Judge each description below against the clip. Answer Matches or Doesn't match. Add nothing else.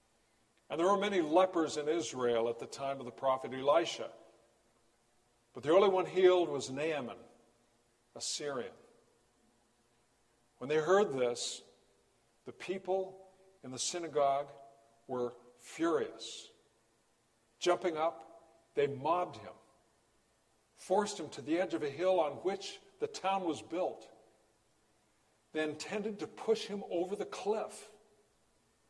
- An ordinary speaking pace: Doesn't match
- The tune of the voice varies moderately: Doesn't match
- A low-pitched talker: Matches